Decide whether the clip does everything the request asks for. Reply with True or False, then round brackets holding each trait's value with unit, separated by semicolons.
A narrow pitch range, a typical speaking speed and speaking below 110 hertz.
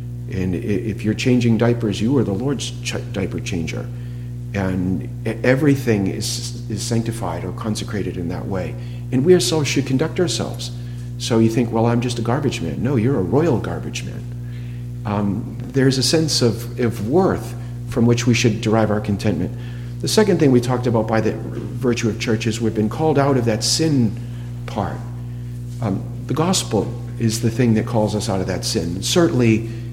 False (1.4 semitones; 185 wpm; 120 Hz)